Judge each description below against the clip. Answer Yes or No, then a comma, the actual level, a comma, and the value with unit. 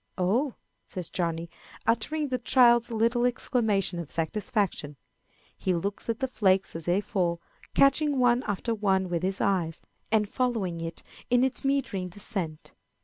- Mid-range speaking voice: No, high, 205 Hz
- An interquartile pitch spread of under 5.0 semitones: No, average, 5.3 semitones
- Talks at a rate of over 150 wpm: No, average, 145 wpm